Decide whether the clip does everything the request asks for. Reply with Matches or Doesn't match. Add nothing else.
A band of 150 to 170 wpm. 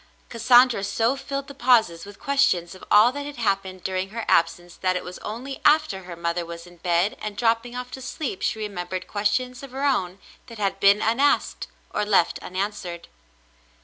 Doesn't match